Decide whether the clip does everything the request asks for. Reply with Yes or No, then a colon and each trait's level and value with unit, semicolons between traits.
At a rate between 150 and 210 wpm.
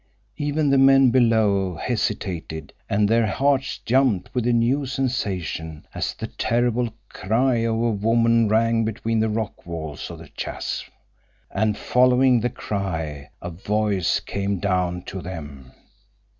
No: average, 140 wpm